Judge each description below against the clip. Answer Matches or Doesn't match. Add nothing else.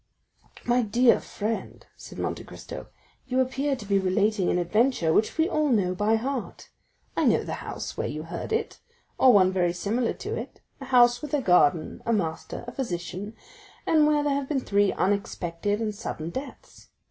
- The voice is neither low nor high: Doesn't match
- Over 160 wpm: Matches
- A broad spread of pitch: Matches